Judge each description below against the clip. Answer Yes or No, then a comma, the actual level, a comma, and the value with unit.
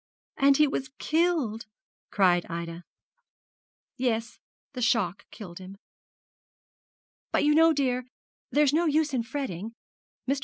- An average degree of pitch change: No, wide, 6.5 semitones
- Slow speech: Yes, slow, 120 wpm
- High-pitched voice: Yes, very high, 250 Hz